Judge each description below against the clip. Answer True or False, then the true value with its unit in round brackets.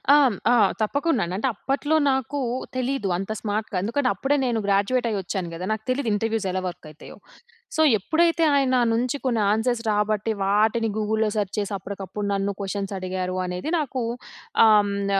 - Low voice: False (215 Hz)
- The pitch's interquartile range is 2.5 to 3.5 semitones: False (4.4 semitones)